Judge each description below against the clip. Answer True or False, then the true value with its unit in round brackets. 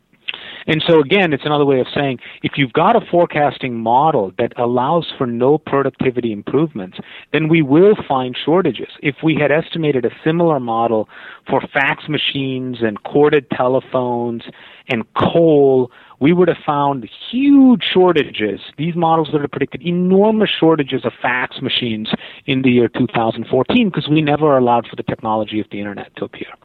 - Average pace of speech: True (160 wpm)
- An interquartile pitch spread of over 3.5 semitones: True (4.7 semitones)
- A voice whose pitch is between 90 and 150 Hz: True (140 Hz)